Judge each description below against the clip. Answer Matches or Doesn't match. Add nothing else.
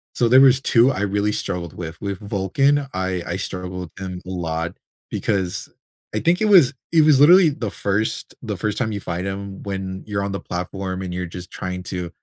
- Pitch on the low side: Matches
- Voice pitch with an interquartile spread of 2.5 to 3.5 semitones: Doesn't match